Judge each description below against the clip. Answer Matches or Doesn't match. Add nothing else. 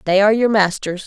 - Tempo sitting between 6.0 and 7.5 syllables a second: Matches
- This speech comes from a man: Doesn't match